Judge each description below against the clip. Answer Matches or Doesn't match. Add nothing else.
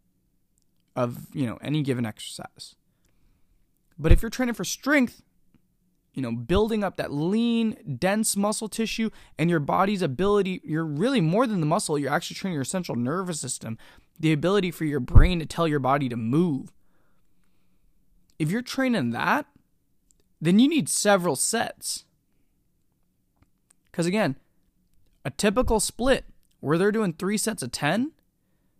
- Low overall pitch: Doesn't match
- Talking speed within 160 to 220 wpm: Doesn't match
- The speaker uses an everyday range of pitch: Doesn't match